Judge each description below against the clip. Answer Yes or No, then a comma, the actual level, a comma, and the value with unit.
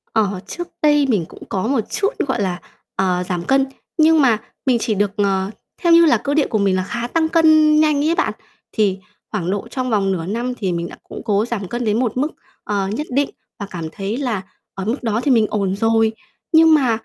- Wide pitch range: Yes, wide, 6.3 semitones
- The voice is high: Yes, high, 225 Hz